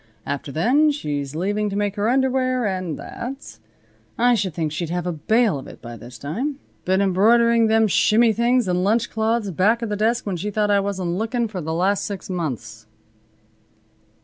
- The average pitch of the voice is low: No, high, 205 Hz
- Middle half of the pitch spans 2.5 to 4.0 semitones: No, average, 5.1 semitones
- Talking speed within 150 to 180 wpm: No, average, 190 wpm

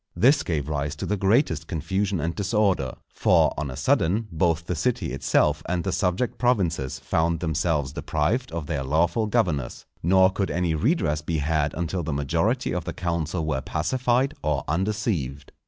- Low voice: Yes, very low, 85 Hz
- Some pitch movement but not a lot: Yes, average, 4.4 semitones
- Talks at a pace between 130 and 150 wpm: No, average, 170 wpm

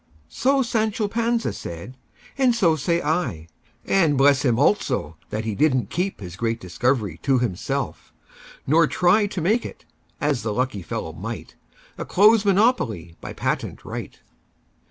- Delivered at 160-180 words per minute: No, slow, 135 wpm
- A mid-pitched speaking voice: Yes, medium, 145 Hz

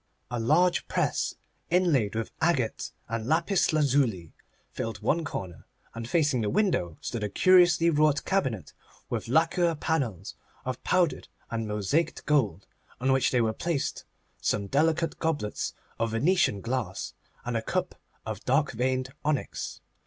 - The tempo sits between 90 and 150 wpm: Yes, average, 140 wpm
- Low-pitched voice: Yes, low, 130 Hz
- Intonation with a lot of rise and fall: Yes, wide, 6.3 semitones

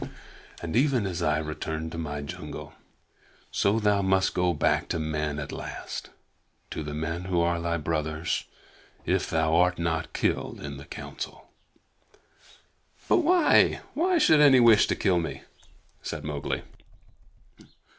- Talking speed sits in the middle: Yes, average, 145 wpm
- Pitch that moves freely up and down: No, average, 3.7 semitones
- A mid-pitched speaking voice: No, very low, 85 Hz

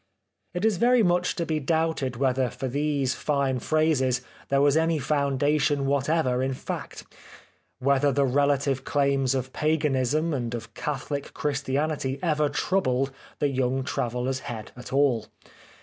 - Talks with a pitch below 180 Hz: Yes, medium, 140 Hz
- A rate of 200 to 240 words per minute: No, average, 140 wpm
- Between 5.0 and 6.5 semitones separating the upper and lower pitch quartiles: No, narrow, 2.6 semitones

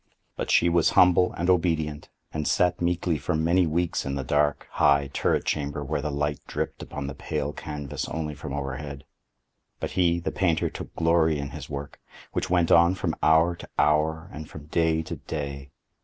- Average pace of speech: Yes, average, 185 wpm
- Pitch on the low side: Yes, very low, 80 Hz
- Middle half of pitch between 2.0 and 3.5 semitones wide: Yes, average, 2.8 semitones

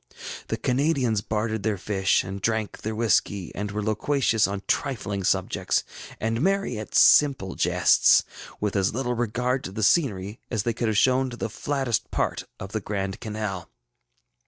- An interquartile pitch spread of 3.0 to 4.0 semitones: Yes, average, 3.6 semitones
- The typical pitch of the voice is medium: No, low, 110 Hz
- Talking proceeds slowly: No, average, 160 wpm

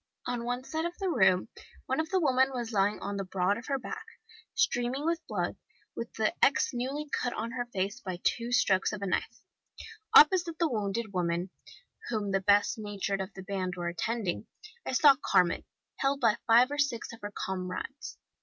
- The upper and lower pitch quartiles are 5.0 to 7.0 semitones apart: Yes, wide, 5.4 semitones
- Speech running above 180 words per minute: Yes, average, 190 wpm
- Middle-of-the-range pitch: No, high, 230 Hz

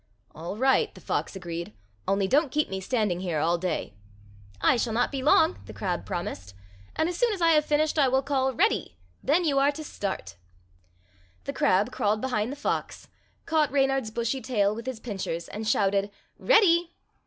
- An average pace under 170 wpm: No, average, 185 wpm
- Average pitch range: No, wide, 6.8 semitones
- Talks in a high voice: Yes, high, 245 Hz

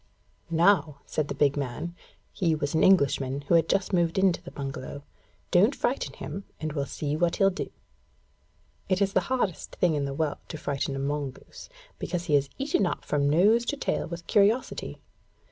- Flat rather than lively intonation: No, average, 5.0 semitones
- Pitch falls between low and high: Yes, medium, 165 Hz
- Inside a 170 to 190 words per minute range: Yes, average, 185 wpm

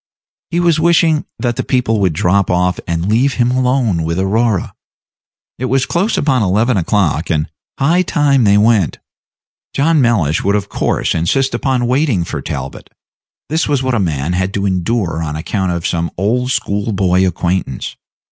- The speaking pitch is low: Yes, low, 105 Hz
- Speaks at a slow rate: No, average, 170 wpm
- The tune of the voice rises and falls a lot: Yes, wide, 6.5 semitones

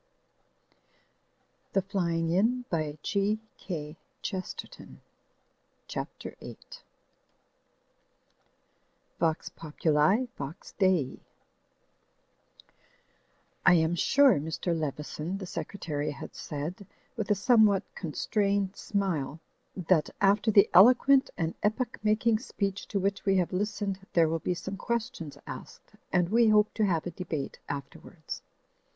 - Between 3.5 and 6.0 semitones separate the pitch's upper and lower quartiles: Yes, average, 4.4 semitones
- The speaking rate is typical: No, slow, 105 wpm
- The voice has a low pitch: No, high, 190 Hz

